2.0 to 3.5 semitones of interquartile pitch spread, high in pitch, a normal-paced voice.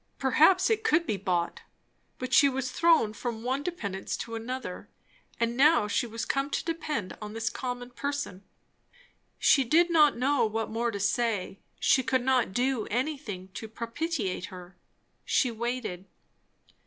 No: average, 4.8 semitones; high, 245 Hz; average, 155 wpm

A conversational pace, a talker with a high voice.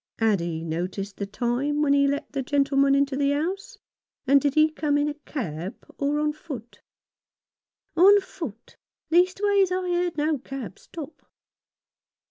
Yes: average, 160 wpm; very high, 285 Hz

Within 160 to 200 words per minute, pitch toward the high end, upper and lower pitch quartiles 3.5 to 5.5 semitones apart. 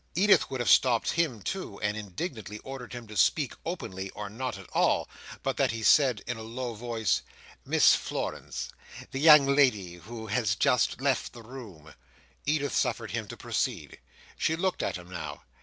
No: average, 170 wpm; low, 120 Hz; average, 4.6 semitones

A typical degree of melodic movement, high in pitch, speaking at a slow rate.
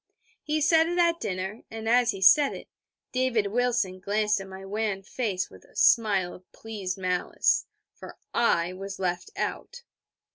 No: average, 4.6 semitones; high, 210 Hz; average, 160 wpm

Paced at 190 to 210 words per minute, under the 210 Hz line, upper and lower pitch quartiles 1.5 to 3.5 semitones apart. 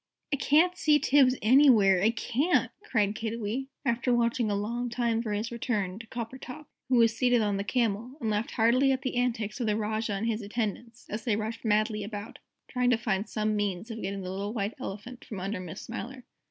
No: fast, 205 wpm; high, 225 Hz; average, 2.9 semitones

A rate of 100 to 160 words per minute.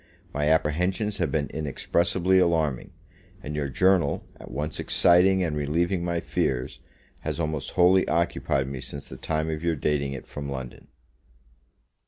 Yes: average, 150 wpm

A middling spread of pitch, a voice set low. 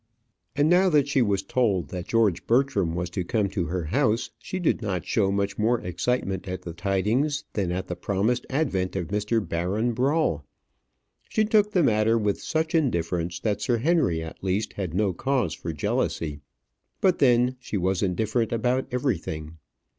No: wide, 5.7 semitones; low, 105 Hz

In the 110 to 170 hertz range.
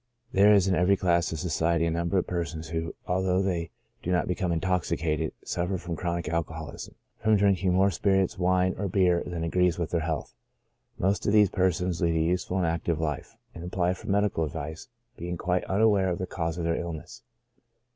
No: very low, 90 Hz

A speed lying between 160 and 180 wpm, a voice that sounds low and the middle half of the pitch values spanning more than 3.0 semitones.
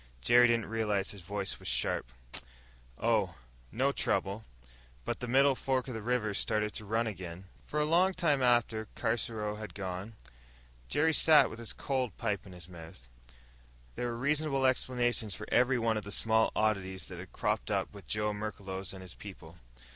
Yes: average, 175 wpm; low, 110 Hz; average, 3.9 semitones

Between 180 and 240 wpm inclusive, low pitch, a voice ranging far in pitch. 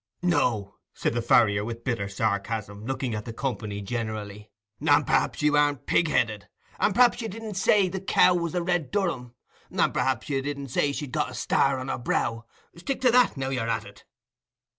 Yes: average, 190 wpm; low, 130 Hz; wide, 7.3 semitones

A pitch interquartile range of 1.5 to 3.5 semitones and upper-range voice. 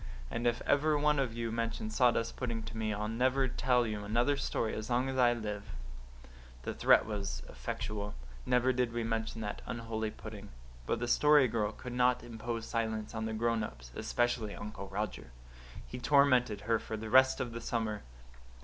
No: narrow, 2.4 semitones; low, 115 Hz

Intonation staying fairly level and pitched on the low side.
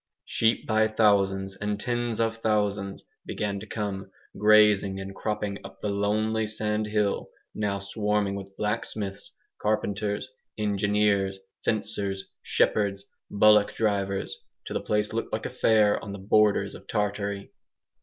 Yes: narrow, 1.4 semitones; low, 105 Hz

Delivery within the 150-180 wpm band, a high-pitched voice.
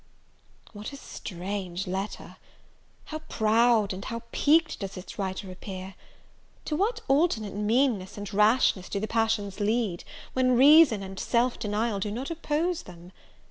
No: average, 140 wpm; high, 215 Hz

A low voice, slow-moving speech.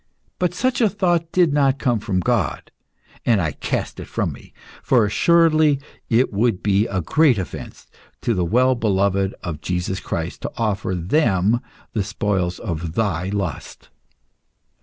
No: low, 105 Hz; average, 155 wpm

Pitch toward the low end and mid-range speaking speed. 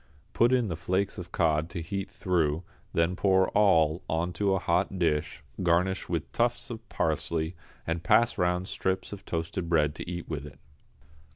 Yes: very low, 90 Hz; average, 175 wpm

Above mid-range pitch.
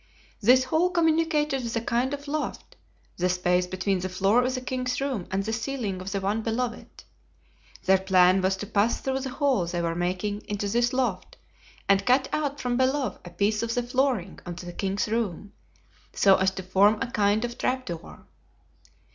Yes: high, 220 Hz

